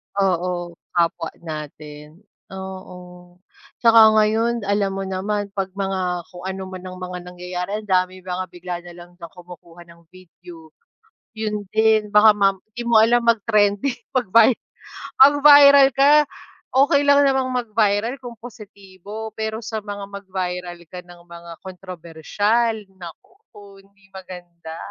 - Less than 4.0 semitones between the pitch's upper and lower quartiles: Yes, average, 3.6 semitones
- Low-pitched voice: No, high, 195 Hz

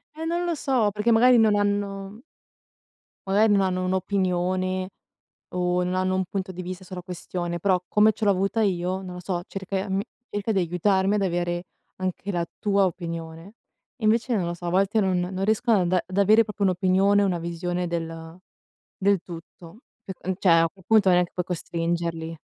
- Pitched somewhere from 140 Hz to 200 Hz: Yes, medium, 185 Hz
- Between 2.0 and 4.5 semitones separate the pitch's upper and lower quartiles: Yes, narrow, 2.4 semitones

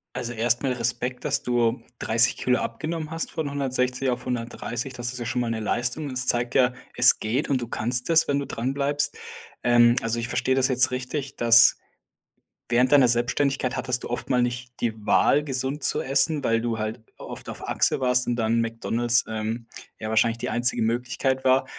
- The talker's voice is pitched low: Yes, low, 125 Hz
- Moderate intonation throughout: No, narrow, 2.0 semitones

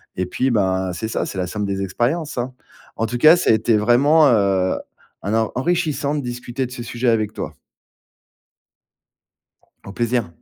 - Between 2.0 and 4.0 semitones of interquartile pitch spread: No, average, 4.4 semitones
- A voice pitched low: Yes, low, 120 Hz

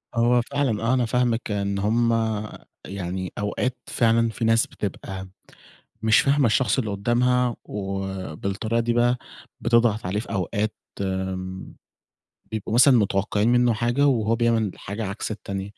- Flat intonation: No, average, 3.2 semitones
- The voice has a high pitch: No, low, 110 Hz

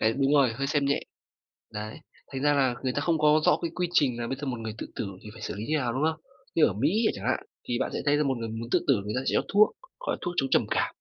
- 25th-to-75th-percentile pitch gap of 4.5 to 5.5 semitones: No, average, 4.1 semitones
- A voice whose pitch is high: No, low, 135 Hz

